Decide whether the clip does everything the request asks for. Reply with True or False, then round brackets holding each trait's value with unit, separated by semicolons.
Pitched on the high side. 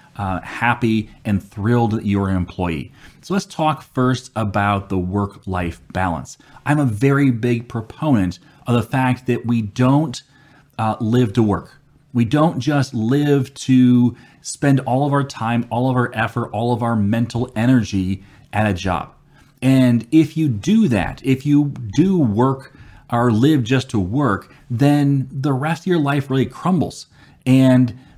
False (125 Hz)